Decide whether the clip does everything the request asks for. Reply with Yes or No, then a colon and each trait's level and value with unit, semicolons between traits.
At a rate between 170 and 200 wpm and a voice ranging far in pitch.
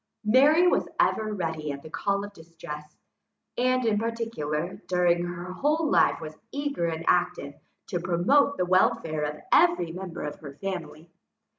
No: average, 155 wpm; wide, 5.9 semitones